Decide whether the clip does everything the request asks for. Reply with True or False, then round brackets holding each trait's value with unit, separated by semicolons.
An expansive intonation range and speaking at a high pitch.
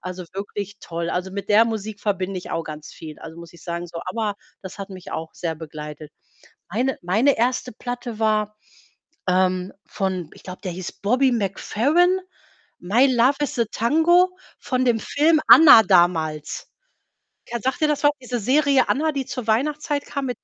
True (6.3 semitones; 215 Hz)